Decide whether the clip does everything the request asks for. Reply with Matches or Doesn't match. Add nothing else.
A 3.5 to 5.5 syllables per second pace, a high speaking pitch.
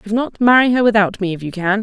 Doesn't match